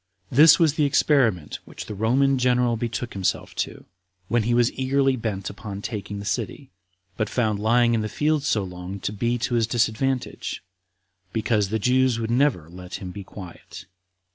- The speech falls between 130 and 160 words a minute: No, average, 175 wpm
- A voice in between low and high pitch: No, low, 115 Hz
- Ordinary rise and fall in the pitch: Yes, average, 4.0 semitones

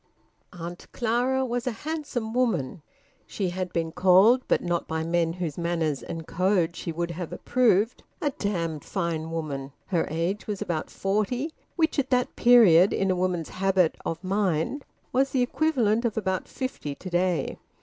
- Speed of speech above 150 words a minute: Yes, average, 165 wpm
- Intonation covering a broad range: Yes, wide, 6.1 semitones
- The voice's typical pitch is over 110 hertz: Yes, medium, 185 Hz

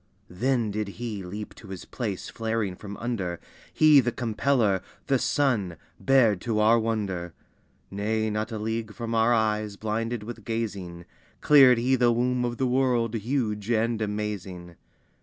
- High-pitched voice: No, low, 110 Hz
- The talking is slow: No, average, 155 wpm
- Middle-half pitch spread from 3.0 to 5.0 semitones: No, narrow, 2.6 semitones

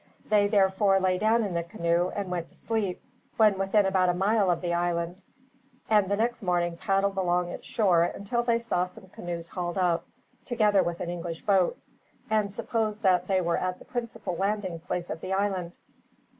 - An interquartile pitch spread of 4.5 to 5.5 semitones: No, average, 2.8 semitones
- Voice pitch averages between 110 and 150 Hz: No, high, 190 Hz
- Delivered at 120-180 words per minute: No, average, 190 wpm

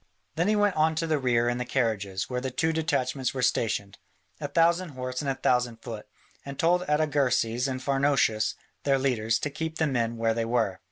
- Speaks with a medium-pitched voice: No, low, 130 Hz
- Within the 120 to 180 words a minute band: No, fast, 205 wpm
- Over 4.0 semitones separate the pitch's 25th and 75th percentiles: Yes, average, 4.5 semitones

